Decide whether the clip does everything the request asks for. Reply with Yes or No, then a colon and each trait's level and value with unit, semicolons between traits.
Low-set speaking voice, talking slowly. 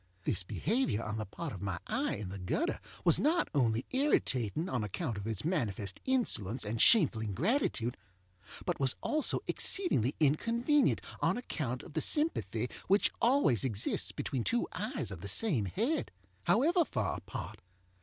No: low, 130 Hz; average, 155 wpm